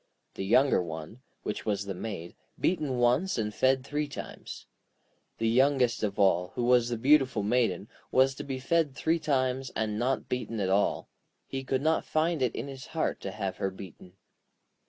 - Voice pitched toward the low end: Yes, low, 125 Hz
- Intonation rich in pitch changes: No, average, 4.5 semitones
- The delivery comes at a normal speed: Yes, average, 180 wpm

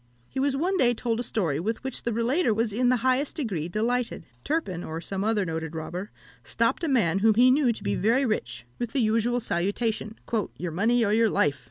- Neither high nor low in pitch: No, high, 225 Hz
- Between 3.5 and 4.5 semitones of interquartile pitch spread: No, average, 5.1 semitones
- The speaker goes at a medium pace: No, fast, 215 wpm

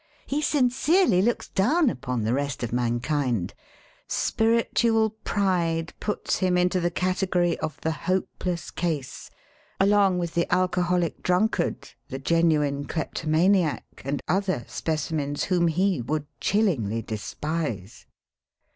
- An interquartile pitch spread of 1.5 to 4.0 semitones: No, average, 5.0 semitones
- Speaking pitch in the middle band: Yes, medium, 170 Hz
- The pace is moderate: No, slow, 125 wpm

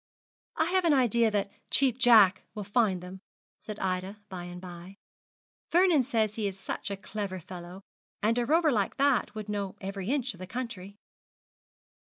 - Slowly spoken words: No, average, 175 wpm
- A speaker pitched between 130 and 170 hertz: No, high, 205 Hz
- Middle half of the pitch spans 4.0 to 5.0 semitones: Yes, average, 4.4 semitones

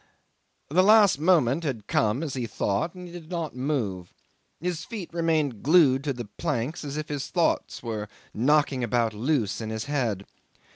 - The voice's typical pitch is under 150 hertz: Yes, medium, 140 Hz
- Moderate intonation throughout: No, wide, 6.1 semitones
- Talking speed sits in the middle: Yes, average, 165 wpm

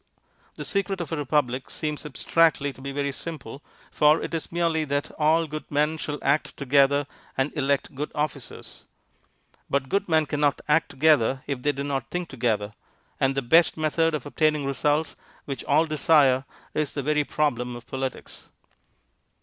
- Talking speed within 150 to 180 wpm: Yes, average, 165 wpm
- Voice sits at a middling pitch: Yes, medium, 145 Hz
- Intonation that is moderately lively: No, narrow, 2.3 semitones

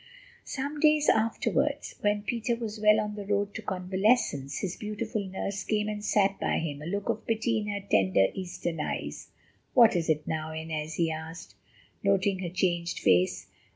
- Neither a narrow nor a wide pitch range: Yes, average, 4.6 semitones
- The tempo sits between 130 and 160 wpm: No, average, 175 wpm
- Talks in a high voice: Yes, high, 195 Hz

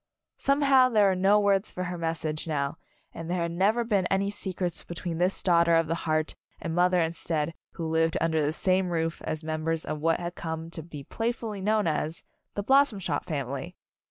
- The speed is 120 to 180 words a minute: No, average, 200 wpm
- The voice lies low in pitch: No, medium, 170 Hz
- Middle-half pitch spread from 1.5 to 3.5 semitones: Yes, average, 3.2 semitones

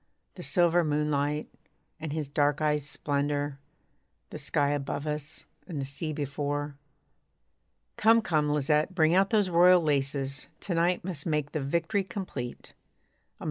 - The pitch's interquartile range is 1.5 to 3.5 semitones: Yes, average, 3.0 semitones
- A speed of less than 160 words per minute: Yes, average, 140 wpm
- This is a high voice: No, medium, 150 Hz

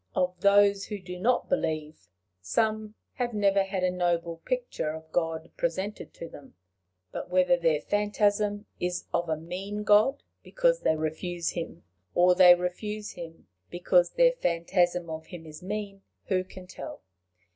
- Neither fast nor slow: Yes, average, 155 wpm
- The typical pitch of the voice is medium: Yes, medium, 180 Hz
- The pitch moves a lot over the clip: No, average, 3.4 semitones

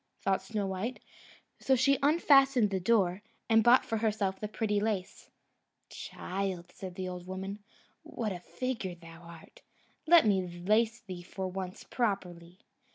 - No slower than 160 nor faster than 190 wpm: No, average, 145 wpm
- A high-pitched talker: Yes, high, 195 Hz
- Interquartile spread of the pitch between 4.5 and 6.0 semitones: No, average, 3.7 semitones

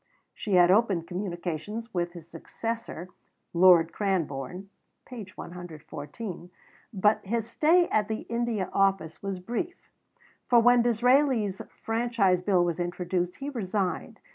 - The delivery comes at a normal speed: No, slow, 120 wpm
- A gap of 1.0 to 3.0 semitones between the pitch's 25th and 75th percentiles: No, average, 4.7 semitones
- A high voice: Yes, high, 195 Hz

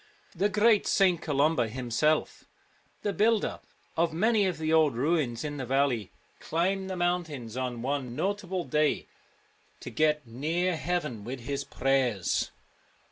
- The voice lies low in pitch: No, medium, 155 Hz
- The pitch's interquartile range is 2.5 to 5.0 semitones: No, wide, 5.5 semitones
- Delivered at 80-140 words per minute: Yes, slow, 135 wpm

